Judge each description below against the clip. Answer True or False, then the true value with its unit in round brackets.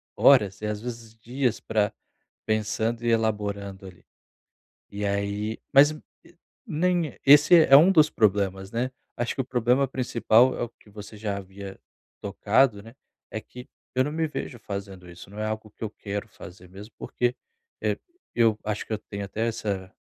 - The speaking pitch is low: True (110 Hz)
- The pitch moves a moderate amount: True (3.5 semitones)